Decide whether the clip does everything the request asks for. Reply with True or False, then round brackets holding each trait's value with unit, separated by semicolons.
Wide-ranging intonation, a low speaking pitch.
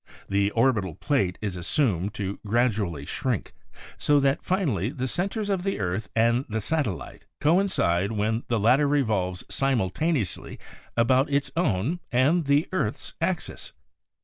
True (6.6 semitones; 120 Hz)